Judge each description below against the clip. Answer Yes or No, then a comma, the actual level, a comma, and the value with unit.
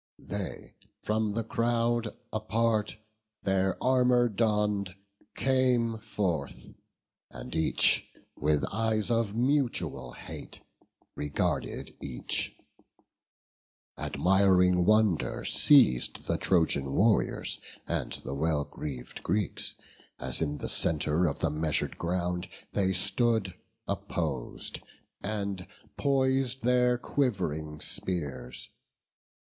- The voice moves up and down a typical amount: No, wide, 6.2 semitones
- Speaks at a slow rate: Yes, slow, 95 wpm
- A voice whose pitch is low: Yes, low, 100 Hz